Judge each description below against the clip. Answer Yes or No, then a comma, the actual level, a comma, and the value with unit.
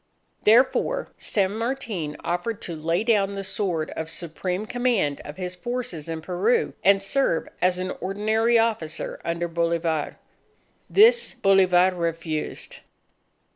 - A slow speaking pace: Yes, slow, 125 wpm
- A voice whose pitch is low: No, medium, 185 Hz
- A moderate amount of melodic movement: Yes, average, 4.8 semitones